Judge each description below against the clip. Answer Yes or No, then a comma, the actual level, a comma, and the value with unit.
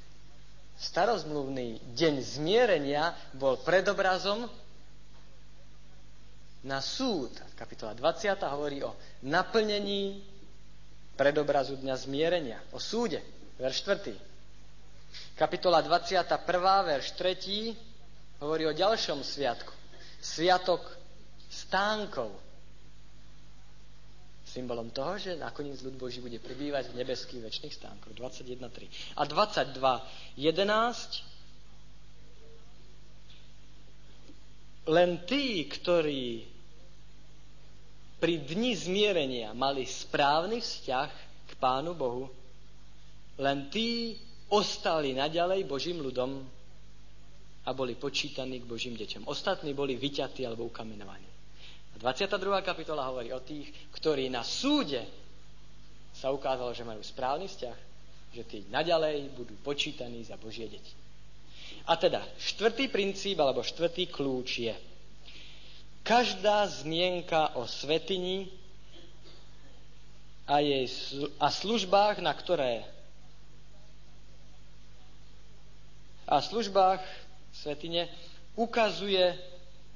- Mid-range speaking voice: Yes, medium, 145 Hz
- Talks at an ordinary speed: No, slow, 90 wpm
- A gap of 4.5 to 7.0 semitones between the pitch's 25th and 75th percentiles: Yes, average, 5.0 semitones